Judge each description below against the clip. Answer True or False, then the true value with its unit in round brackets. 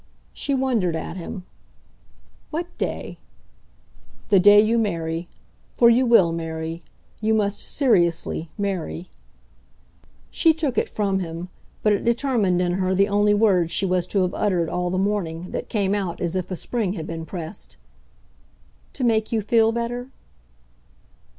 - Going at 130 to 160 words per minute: True (150 wpm)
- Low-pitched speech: False (195 Hz)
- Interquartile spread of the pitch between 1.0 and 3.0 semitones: False (4.2 semitones)